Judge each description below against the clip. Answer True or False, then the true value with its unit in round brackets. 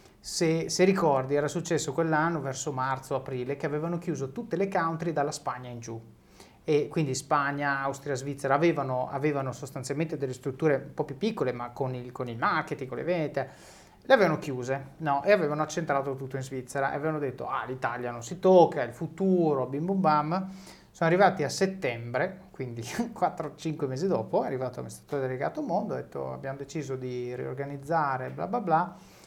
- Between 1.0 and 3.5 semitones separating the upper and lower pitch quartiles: False (3.9 semitones)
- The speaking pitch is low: False (145 Hz)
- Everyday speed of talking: False (180 wpm)